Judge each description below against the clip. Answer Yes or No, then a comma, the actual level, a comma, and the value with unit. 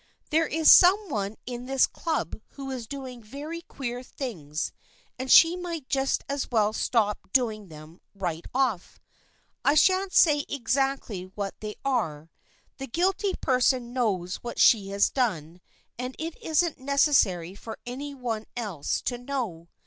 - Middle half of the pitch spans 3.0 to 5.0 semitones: No, wide, 5.5 semitones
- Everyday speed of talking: Yes, average, 150 wpm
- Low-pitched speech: No, very high, 250 Hz